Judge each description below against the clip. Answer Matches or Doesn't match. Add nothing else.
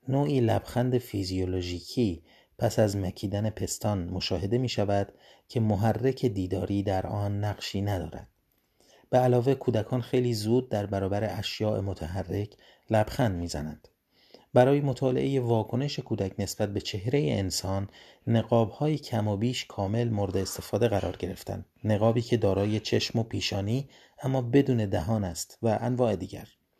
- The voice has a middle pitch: Doesn't match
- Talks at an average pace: Matches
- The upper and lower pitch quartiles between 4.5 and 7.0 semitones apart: Doesn't match